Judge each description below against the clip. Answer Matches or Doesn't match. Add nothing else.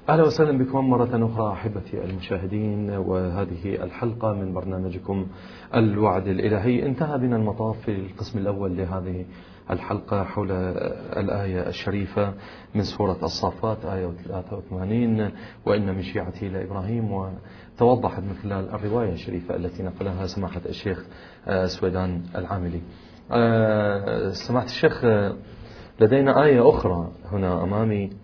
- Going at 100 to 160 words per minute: Matches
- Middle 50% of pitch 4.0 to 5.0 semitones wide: Doesn't match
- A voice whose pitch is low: Matches